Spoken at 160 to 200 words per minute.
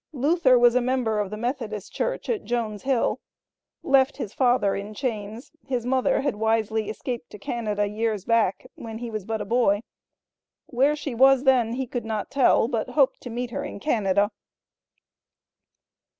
Yes: average, 170 wpm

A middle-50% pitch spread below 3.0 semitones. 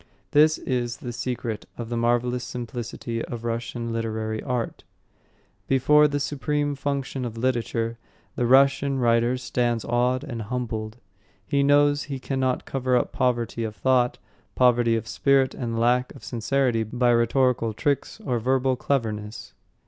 Yes: narrow, 2.4 semitones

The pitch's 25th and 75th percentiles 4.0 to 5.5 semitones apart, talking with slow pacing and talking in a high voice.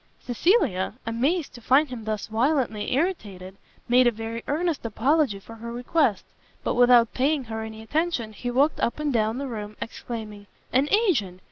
No: average, 4.6 semitones; average, 165 wpm; high, 240 Hz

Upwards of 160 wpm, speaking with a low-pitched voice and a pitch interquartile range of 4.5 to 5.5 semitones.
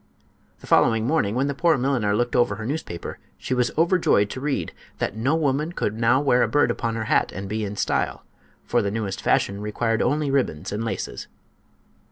Yes: average, 200 wpm; low, 120 Hz; average, 4.8 semitones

